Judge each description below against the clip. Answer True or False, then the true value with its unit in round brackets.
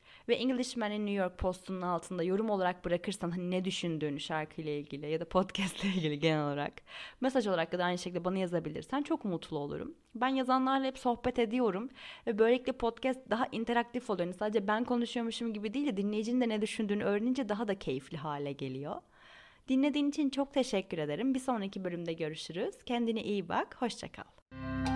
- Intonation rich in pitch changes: True (6.0 semitones)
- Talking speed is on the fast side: True (175 wpm)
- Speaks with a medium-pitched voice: False (205 Hz)